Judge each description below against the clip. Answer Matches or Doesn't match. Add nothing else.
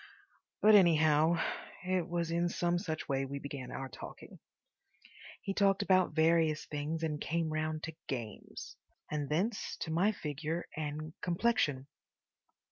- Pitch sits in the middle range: Matches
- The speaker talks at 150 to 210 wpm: Doesn't match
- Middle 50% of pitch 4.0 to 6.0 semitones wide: Doesn't match